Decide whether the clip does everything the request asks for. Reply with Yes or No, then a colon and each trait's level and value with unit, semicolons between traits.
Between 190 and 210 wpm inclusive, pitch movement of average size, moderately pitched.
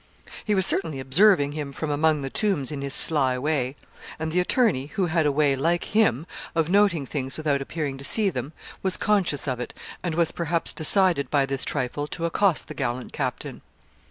Yes: average, 195 wpm; average, 4.1 semitones; medium, 155 Hz